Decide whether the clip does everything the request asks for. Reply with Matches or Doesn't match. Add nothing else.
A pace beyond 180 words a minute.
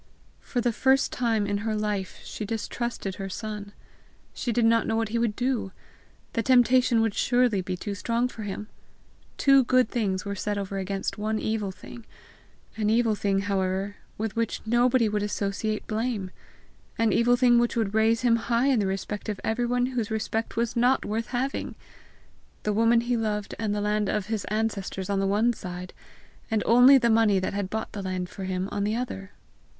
Matches